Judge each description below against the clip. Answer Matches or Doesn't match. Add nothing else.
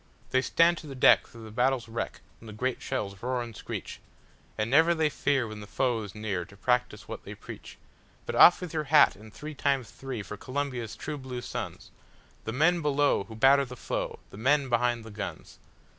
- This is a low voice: Matches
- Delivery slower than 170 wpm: Doesn't match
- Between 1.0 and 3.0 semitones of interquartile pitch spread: Doesn't match